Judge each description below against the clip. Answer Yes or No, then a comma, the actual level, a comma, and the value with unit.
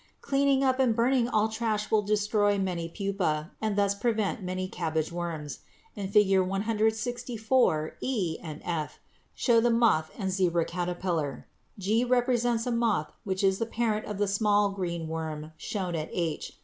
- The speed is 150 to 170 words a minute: Yes, average, 160 wpm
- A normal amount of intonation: Yes, average, 4.6 semitones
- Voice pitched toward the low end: No, high, 200 Hz